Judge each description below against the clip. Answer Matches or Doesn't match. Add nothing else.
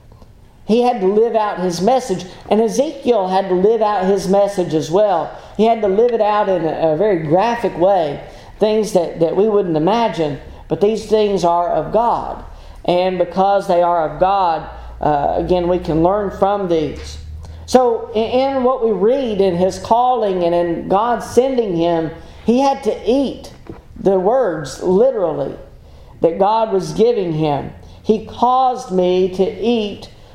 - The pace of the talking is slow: Doesn't match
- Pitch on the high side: Matches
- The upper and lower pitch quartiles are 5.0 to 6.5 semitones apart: Doesn't match